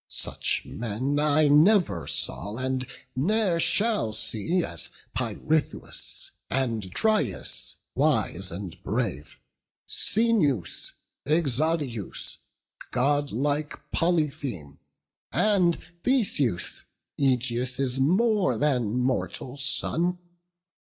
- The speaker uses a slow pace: Yes, slow, 80 wpm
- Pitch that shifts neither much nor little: No, wide, 6.2 semitones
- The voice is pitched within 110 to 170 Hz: Yes, low, 135 Hz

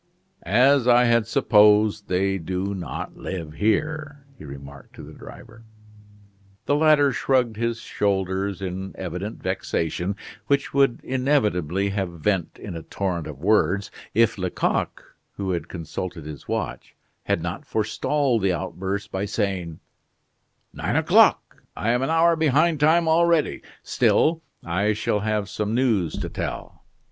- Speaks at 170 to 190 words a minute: No, average, 140 wpm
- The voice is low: Yes, low, 105 Hz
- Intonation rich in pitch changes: Yes, wide, 5.7 semitones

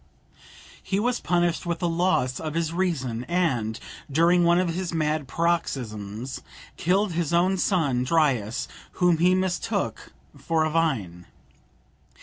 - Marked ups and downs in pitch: No, average, 5.0 semitones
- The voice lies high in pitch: No, medium, 165 Hz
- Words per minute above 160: No, slow, 135 wpm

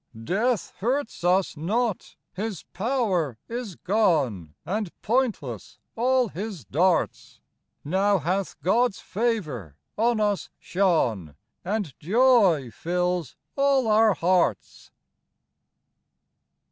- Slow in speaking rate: Yes, slow, 95 wpm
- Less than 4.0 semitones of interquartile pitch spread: No, average, 5.1 semitones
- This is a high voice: Yes, high, 195 Hz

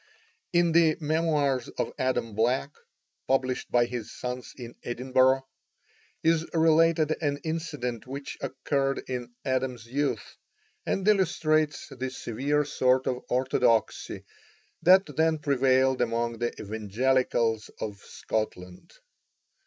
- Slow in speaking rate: Yes, slow, 110 wpm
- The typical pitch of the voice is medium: No, low, 130 Hz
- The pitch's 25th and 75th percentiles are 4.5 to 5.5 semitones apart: No, average, 4.0 semitones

